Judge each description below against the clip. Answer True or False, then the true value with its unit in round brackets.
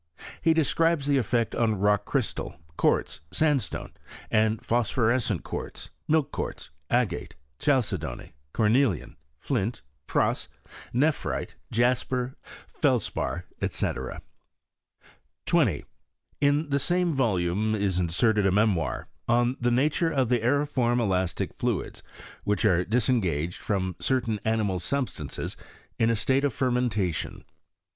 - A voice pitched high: False (120 Hz)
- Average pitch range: True (4.5 semitones)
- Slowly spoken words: True (115 wpm)